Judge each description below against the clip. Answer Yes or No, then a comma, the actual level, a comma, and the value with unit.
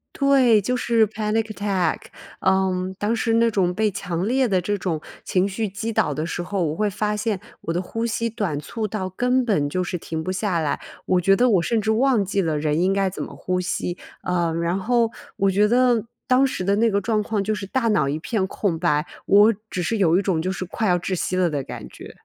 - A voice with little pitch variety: No, average, 3.6 semitones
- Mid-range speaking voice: No, high, 195 Hz